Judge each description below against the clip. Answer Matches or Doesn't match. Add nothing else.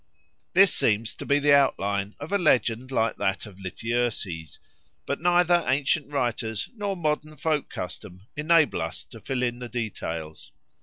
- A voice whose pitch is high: Doesn't match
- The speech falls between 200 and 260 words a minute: Doesn't match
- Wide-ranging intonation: Matches